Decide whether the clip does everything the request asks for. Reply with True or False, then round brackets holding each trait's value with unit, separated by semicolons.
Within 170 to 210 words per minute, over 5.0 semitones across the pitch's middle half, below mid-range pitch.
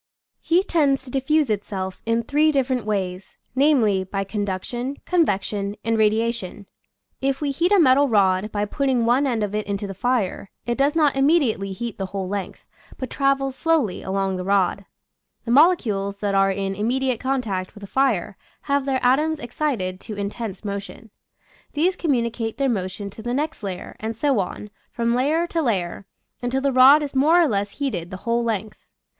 False (180 wpm; 5.5 semitones; 230 Hz)